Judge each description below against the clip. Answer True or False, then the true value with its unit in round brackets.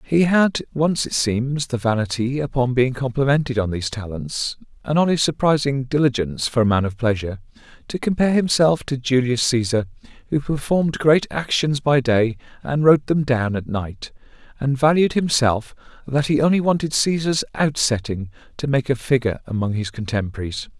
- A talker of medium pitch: False (130 Hz)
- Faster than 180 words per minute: False (165 wpm)